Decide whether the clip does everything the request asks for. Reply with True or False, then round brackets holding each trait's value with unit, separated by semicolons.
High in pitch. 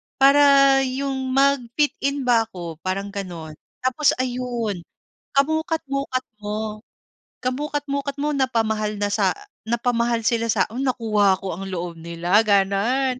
True (235 Hz)